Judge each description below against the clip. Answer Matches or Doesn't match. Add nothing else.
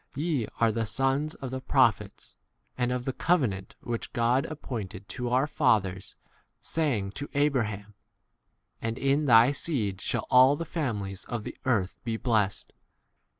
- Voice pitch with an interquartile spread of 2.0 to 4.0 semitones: Doesn't match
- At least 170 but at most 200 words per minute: Doesn't match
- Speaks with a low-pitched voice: Matches